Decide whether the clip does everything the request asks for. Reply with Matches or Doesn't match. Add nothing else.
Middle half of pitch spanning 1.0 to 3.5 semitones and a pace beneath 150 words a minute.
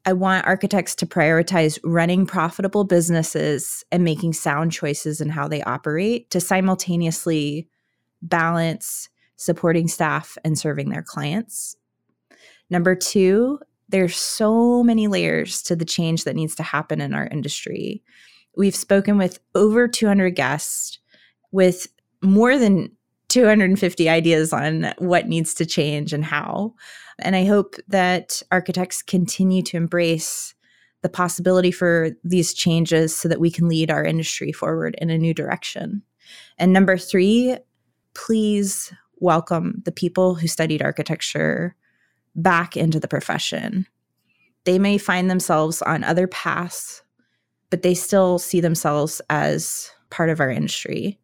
Matches